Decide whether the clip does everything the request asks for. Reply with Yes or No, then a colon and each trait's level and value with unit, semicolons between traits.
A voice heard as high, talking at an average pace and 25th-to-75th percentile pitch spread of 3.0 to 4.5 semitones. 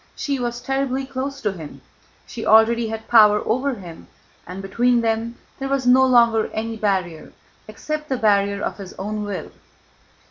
Yes: high, 225 Hz; average, 165 wpm; average, 3.8 semitones